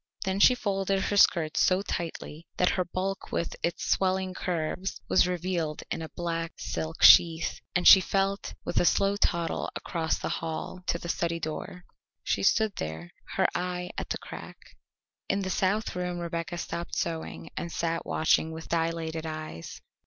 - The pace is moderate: Yes, average, 165 wpm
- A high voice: No, medium, 175 Hz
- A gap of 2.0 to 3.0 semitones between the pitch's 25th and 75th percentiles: Yes, narrow, 2.5 semitones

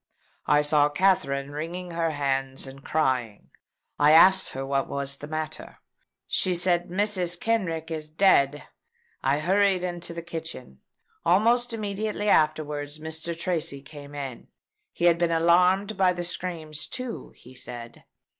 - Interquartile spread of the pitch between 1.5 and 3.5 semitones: No, average, 3.9 semitones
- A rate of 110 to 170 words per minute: Yes, average, 140 wpm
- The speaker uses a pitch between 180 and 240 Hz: No, medium, 160 Hz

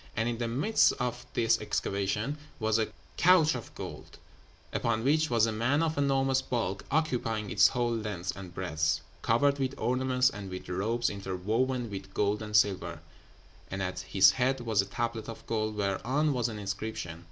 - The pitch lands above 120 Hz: No, low, 115 Hz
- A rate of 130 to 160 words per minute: No, average, 175 wpm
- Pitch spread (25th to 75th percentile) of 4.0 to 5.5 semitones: Yes, average, 4.4 semitones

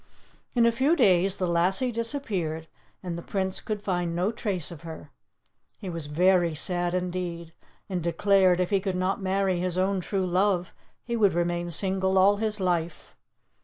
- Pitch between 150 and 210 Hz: Yes, medium, 185 Hz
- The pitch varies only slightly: Yes, narrow, 2.3 semitones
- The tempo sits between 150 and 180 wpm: Yes, average, 170 wpm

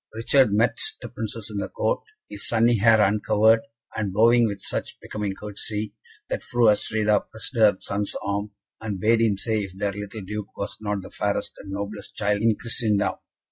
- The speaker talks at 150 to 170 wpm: No, average, 180 wpm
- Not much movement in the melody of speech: Yes, narrow, 1.7 semitones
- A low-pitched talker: Yes, low, 105 Hz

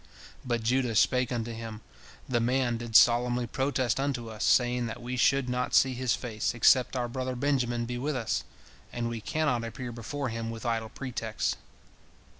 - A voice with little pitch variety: Yes, narrow, 1.8 semitones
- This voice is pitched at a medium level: No, low, 120 Hz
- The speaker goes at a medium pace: Yes, average, 175 wpm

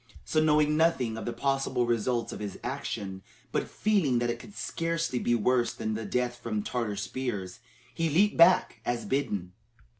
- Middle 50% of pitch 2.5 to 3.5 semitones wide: No, average, 5.2 semitones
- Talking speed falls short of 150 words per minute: No, average, 170 wpm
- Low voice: Yes, low, 125 Hz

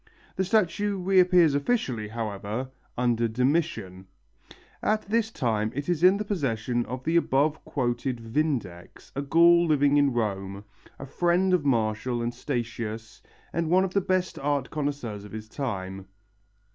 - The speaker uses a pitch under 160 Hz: Yes, low, 135 Hz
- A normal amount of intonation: No, wide, 7.2 semitones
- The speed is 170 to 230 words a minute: No, average, 145 wpm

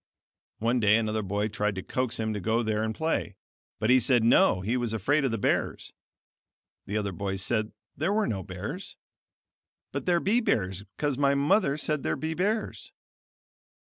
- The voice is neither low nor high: No, low, 115 Hz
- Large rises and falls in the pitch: Yes, wide, 5.8 semitones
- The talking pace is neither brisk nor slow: Yes, average, 180 wpm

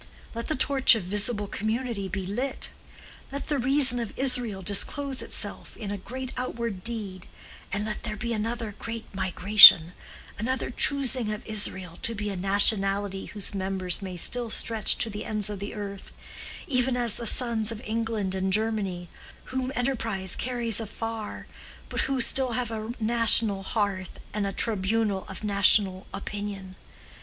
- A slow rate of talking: No, average, 155 wpm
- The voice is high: Yes, high, 215 Hz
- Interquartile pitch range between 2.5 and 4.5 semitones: Yes, average, 3.2 semitones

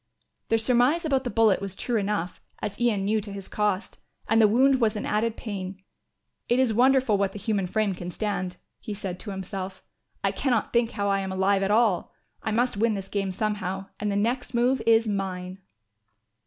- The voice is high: Yes, high, 210 Hz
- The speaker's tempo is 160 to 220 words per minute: Yes, average, 200 wpm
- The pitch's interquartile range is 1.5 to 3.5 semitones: Yes, average, 3.0 semitones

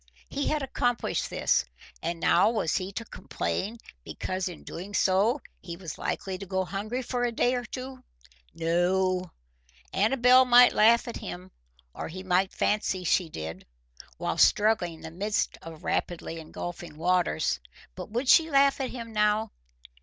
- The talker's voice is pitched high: Yes, high, 195 Hz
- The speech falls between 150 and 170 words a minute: Yes, average, 160 wpm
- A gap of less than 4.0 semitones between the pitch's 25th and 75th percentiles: No, wide, 5.6 semitones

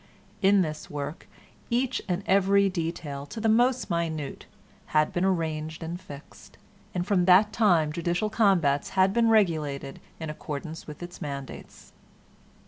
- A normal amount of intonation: Yes, average, 4.5 semitones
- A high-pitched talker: No, medium, 175 Hz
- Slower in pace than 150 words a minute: Yes, average, 140 wpm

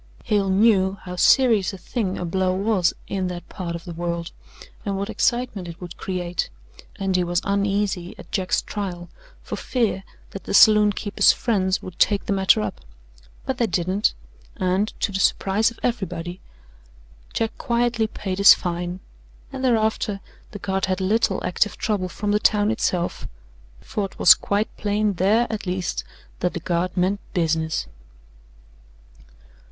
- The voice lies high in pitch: Yes, high, 195 Hz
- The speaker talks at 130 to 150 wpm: No, average, 160 wpm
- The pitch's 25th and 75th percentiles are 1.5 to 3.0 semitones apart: Yes, average, 2.7 semitones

